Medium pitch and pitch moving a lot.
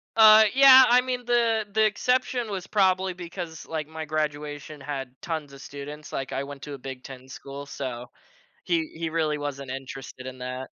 Yes: medium, 150 Hz; wide, 6.1 semitones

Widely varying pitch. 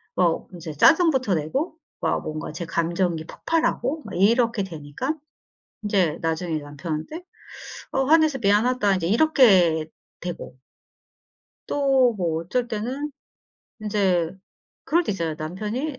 Yes: wide, 7.8 semitones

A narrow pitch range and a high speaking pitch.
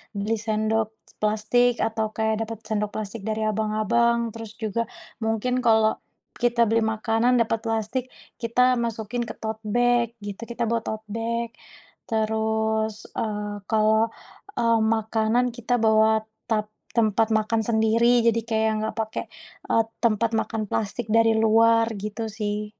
Yes: narrow, 1.1 semitones; high, 220 Hz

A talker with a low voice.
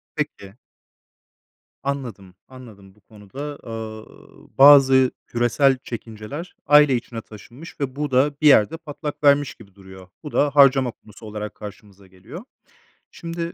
Yes: low, 130 Hz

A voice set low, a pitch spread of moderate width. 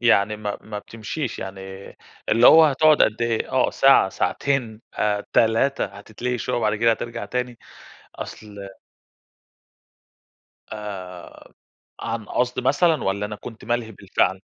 Yes: low, 115 Hz; average, 3.0 semitones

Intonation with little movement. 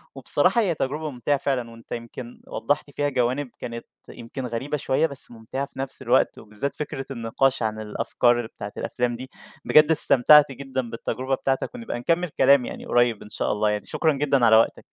No: average, 3.3 semitones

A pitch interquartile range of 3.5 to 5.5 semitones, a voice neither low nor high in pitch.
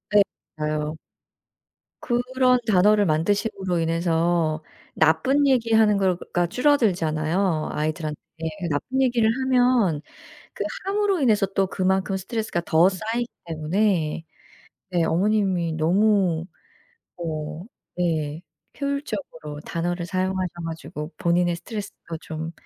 Yes: average, 5.1 semitones; medium, 180 Hz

